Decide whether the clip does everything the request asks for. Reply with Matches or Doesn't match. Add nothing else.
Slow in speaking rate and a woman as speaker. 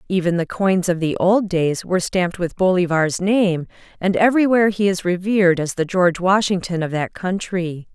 Doesn't match